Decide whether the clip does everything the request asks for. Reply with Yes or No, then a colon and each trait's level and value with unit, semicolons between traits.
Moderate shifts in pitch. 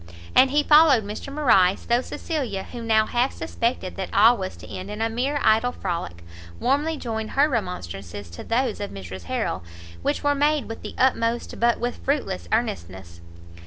No: wide, 6.3 semitones